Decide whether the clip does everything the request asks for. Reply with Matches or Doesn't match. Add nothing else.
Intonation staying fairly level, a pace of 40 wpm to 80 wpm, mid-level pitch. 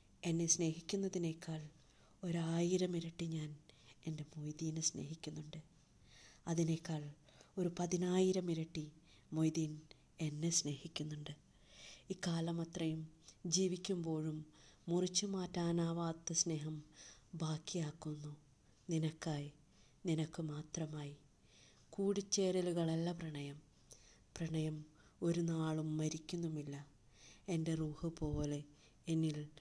Matches